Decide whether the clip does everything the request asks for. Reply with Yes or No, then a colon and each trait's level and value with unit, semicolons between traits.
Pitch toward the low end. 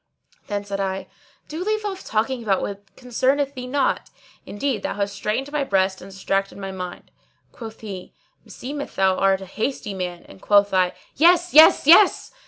No: high, 205 Hz